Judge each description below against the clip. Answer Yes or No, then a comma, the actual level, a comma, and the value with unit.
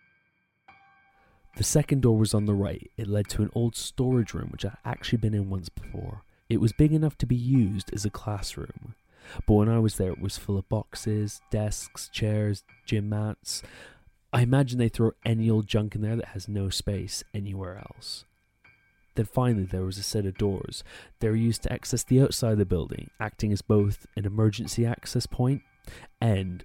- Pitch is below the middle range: Yes, low, 110 Hz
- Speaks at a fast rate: No, average, 195 wpm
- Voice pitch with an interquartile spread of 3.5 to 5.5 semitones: No, average, 2.8 semitones